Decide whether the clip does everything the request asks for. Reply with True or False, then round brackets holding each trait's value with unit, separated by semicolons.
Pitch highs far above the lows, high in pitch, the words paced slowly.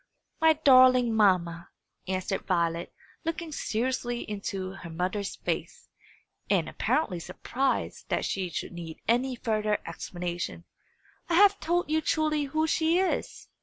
True (8.9 semitones; 225 Hz; 130 wpm)